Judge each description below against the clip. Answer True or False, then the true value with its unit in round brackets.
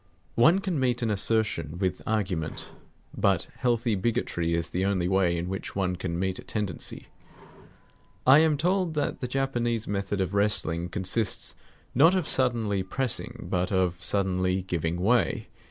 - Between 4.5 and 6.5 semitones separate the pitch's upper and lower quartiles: True (4.9 semitones)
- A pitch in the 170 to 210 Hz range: False (100 Hz)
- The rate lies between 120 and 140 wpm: False (155 wpm)